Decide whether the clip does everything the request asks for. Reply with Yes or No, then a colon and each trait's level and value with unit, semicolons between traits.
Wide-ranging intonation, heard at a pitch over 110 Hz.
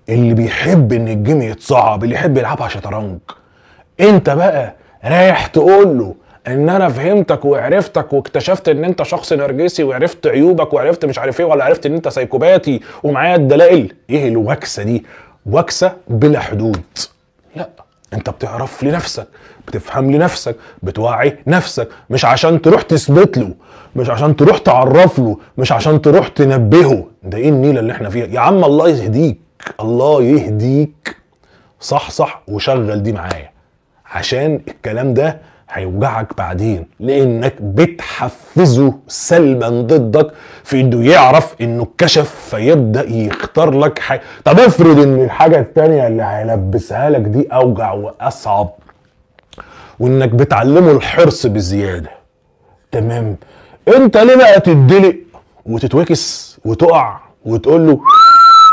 Yes: wide, 6.1 semitones; low, 135 Hz